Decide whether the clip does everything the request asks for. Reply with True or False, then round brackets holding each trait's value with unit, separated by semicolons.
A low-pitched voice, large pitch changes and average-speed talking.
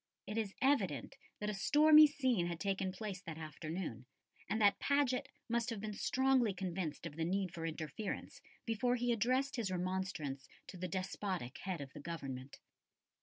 False (190 Hz; 5.8 semitones; 170 wpm)